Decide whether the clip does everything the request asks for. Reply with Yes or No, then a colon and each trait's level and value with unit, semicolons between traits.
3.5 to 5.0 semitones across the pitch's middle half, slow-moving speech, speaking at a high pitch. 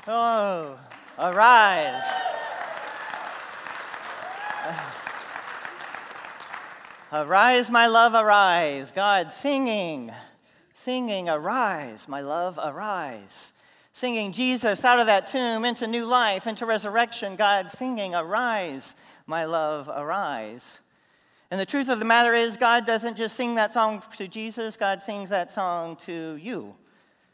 Yes: average, 4.0 semitones; slow, 115 wpm; high, 215 Hz